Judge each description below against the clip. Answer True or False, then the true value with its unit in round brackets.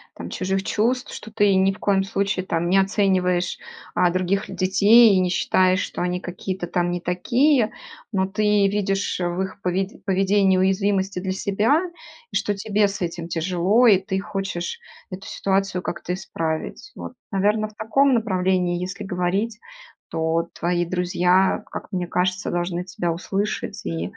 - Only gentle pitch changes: True (2.1 semitones)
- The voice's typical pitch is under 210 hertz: True (190 Hz)